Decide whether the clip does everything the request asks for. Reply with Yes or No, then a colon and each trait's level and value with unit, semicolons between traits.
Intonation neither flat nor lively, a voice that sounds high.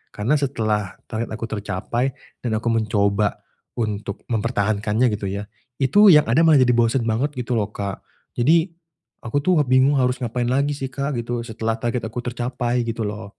No: average, 3.2 semitones; low, 120 Hz